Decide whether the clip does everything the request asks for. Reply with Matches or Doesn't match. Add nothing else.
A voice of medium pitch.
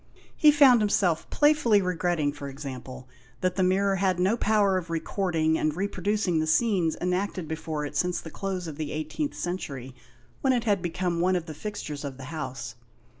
Matches